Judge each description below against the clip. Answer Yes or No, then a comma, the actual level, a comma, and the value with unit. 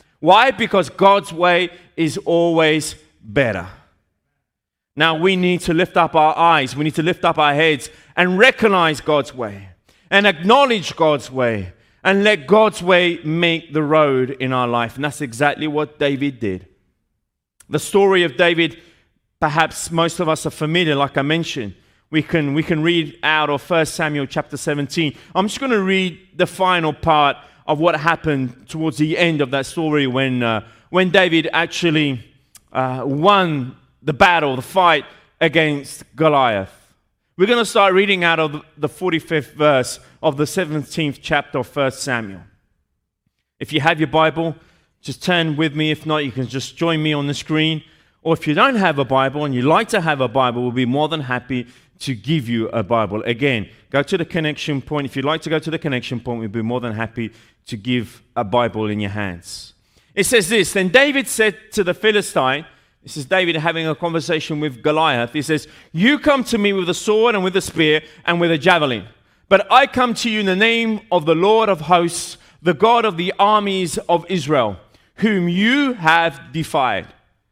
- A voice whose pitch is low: No, medium, 155 Hz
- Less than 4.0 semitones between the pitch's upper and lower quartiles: No, average, 4.5 semitones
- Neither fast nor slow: No, fast, 190 wpm